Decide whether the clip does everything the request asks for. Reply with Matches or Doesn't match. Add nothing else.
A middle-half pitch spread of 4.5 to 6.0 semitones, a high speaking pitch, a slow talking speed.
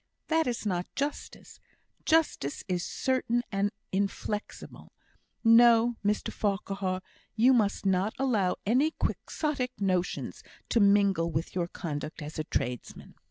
Matches